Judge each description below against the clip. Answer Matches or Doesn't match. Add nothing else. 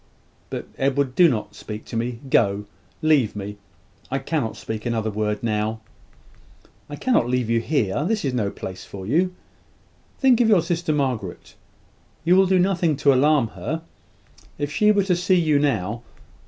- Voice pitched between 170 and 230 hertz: Doesn't match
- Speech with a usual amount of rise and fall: Doesn't match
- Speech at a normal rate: Matches